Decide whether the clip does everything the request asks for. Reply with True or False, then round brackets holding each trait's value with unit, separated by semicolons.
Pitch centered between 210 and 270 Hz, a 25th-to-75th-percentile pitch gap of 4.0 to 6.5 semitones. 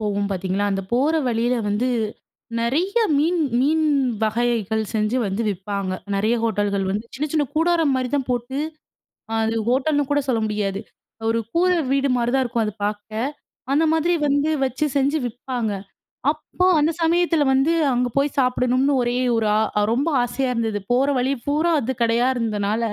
True (245 Hz; 4.7 semitones)